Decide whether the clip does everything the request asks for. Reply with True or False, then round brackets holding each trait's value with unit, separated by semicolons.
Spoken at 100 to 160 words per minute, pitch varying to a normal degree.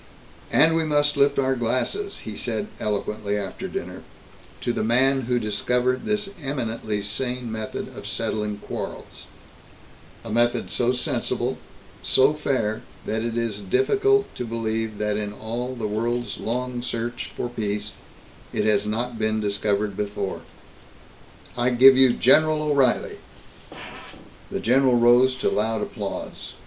True (135 wpm; 3.4 semitones)